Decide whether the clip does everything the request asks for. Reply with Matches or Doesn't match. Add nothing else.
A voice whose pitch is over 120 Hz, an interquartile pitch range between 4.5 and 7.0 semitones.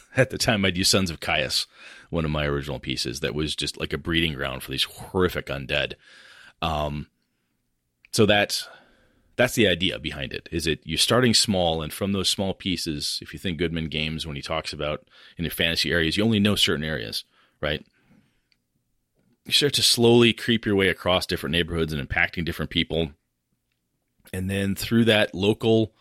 Doesn't match